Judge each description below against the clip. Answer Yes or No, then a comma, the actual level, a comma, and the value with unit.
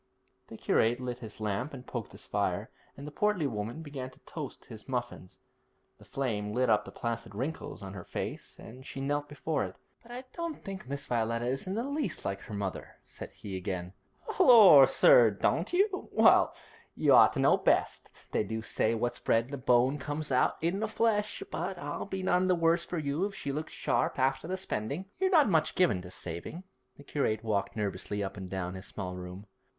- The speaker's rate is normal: No, fast, 210 wpm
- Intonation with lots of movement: Yes, wide, 7.7 semitones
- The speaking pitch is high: No, low, 130 Hz